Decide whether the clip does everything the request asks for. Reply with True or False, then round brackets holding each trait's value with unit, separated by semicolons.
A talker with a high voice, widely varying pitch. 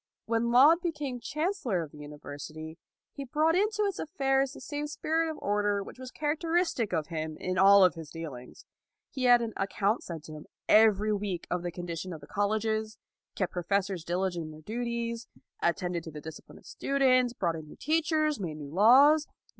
True (210 Hz; 8.1 semitones)